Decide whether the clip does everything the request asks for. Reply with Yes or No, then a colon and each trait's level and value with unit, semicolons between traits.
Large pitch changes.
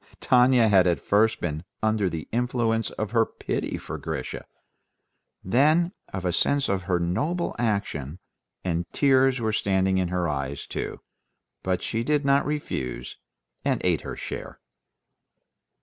Yes: wide, 5.9 semitones